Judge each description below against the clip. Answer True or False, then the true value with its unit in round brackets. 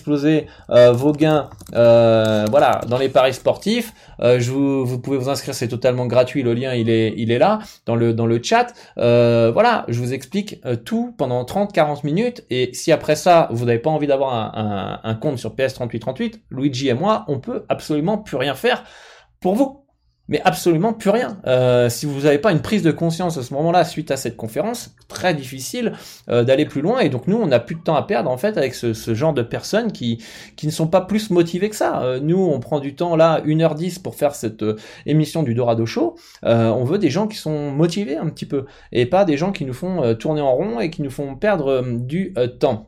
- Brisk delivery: True (230 wpm)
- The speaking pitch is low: False (145 Hz)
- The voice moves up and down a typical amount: False (6.3 semitones)